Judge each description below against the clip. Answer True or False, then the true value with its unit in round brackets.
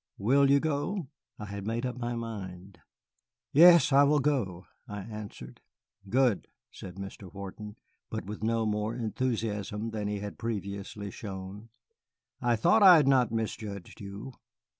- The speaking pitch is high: False (110 Hz)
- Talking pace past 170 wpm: False (145 wpm)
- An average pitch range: True (4.1 semitones)